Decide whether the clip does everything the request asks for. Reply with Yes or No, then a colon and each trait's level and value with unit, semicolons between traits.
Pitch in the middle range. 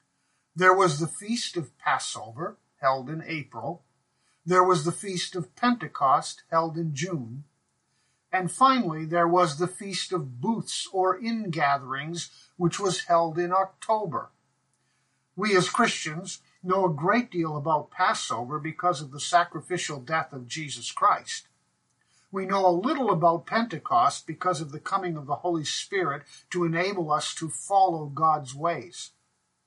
Yes: medium, 170 Hz